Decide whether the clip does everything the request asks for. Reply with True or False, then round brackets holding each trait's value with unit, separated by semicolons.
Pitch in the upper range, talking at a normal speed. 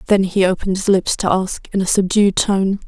False (195 Hz; 230 wpm)